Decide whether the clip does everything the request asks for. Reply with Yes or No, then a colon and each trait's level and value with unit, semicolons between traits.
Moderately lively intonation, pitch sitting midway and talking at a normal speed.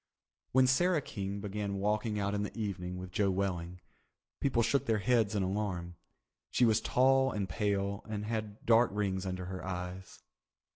No: average, 3.0 semitones; low, 100 Hz; average, 165 wpm